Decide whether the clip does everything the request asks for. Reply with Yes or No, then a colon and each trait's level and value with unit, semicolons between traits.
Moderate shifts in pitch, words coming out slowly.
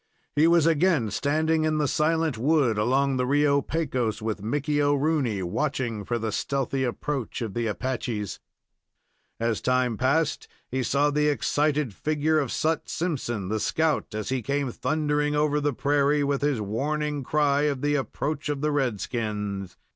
No: average, 4.0 semitones; average, 160 wpm